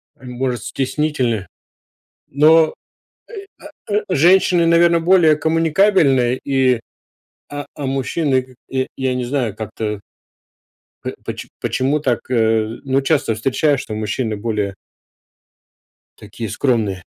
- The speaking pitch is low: Yes, low, 130 Hz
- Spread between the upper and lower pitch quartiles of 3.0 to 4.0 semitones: No, average, 5.1 semitones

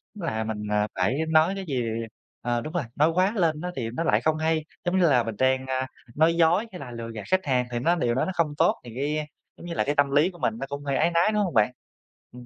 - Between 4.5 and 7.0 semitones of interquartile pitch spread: Yes, average, 5.2 semitones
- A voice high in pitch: No, medium, 145 Hz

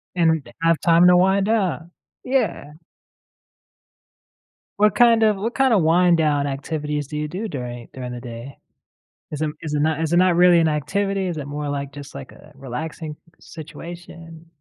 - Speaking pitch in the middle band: Yes, medium, 160 Hz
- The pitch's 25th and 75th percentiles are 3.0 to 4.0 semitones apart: Yes, average, 3.7 semitones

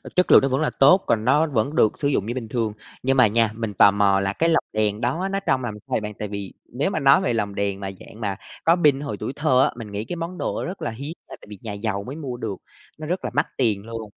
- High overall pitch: No, low, 120 Hz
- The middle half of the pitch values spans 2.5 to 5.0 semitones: No, wide, 5.5 semitones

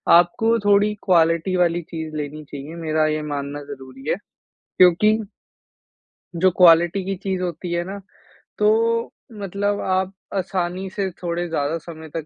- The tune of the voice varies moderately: Yes, average, 3.4 semitones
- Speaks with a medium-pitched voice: Yes, medium, 175 Hz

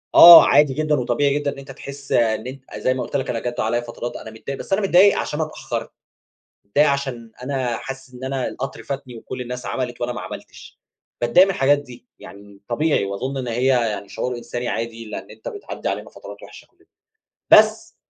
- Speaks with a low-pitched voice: Yes, low, 130 Hz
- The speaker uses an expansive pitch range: No, average, 2.8 semitones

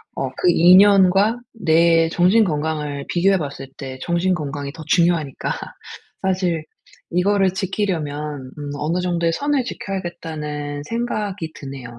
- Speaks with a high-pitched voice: No, medium, 170 Hz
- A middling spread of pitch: Yes, average, 4.3 semitones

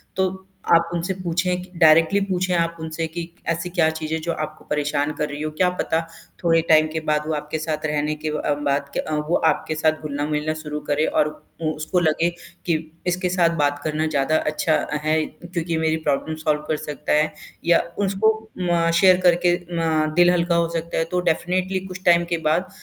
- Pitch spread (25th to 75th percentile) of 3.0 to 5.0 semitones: No, narrow, 2.4 semitones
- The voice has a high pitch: No, medium, 160 Hz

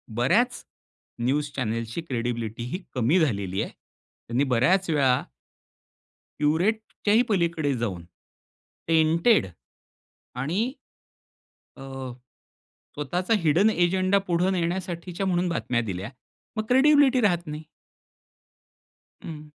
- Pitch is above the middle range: No, medium, 165 Hz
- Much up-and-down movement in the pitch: Yes, wide, 6.8 semitones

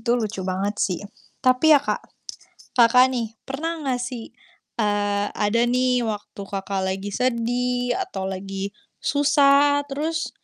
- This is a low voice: No, high, 235 Hz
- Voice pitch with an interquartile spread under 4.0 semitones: No, average, 4.6 semitones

